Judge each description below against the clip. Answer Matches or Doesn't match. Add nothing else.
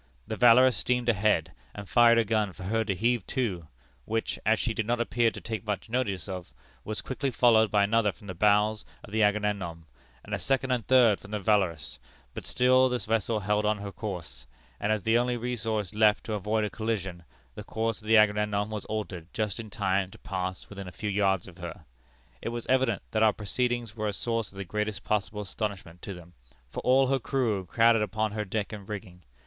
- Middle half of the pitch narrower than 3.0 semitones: Matches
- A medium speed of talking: Doesn't match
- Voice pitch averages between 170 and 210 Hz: Doesn't match